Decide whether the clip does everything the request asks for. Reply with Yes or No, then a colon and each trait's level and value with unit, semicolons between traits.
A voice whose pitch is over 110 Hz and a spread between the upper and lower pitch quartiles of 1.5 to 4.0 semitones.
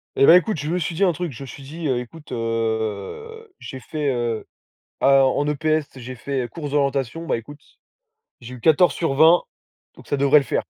No: medium, 140 Hz; average, 4.5 semitones